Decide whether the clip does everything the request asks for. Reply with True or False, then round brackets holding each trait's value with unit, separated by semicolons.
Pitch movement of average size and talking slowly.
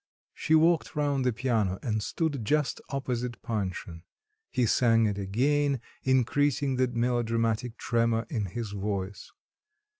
True (3.8 semitones; 125 wpm)